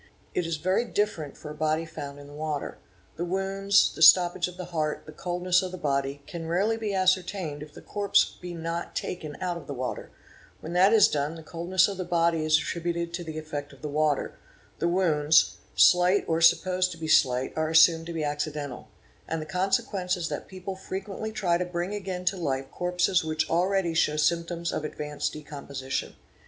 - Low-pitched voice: No, medium, 170 Hz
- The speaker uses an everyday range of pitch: Yes, average, 3.1 semitones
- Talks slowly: No, average, 200 wpm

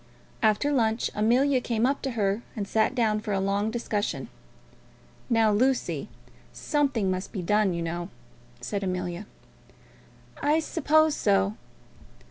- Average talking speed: No, slow, 130 wpm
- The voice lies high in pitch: Yes, high, 215 Hz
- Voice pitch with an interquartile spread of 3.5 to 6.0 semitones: Yes, average, 4.3 semitones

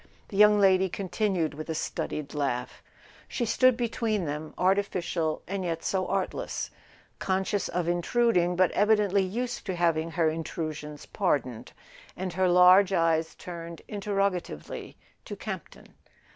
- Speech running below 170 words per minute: Yes, average, 140 wpm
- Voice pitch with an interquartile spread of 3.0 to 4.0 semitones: Yes, average, 3.5 semitones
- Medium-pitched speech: Yes, medium, 180 Hz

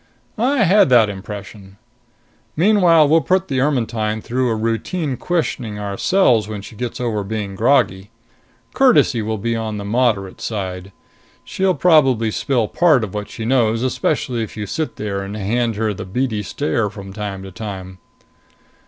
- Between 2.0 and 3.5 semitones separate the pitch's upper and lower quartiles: No, average, 4.5 semitones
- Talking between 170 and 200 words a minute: No, average, 160 wpm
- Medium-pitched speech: No, low, 115 Hz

